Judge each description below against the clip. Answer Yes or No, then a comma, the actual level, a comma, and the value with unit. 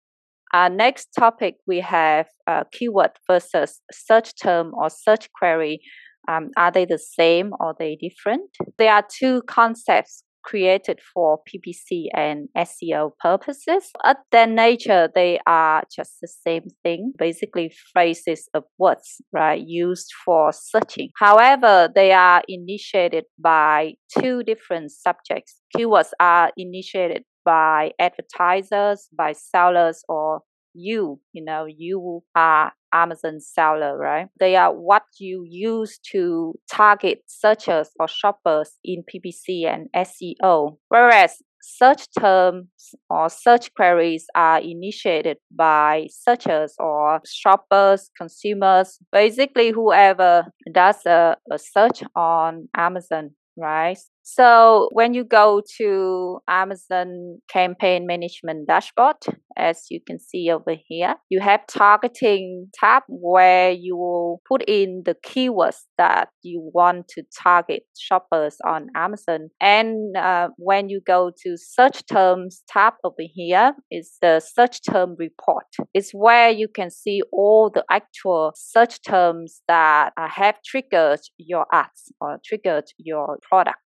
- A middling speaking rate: No, slow, 125 wpm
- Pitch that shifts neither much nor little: Yes, average, 4.3 semitones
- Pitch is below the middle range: No, medium, 185 Hz